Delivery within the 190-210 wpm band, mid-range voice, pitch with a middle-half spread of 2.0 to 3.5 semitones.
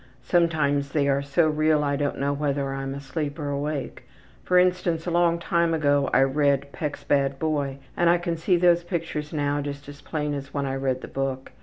Yes: fast, 205 wpm; medium, 145 Hz; average, 2.7 semitones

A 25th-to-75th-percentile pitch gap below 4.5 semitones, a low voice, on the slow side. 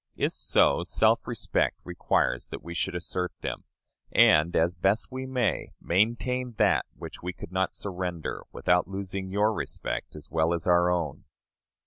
No: average, 3.3 semitones; very low, 90 Hz; average, 155 wpm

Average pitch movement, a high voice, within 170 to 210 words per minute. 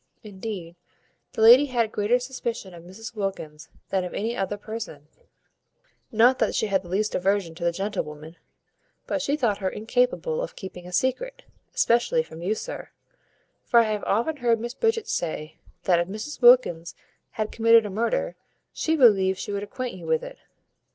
Yes: average, 4.6 semitones; high, 215 Hz; average, 180 wpm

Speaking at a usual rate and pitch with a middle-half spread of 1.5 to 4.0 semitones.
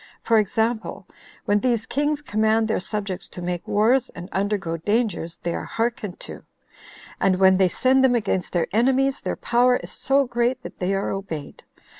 No: average, 175 wpm; average, 4.4 semitones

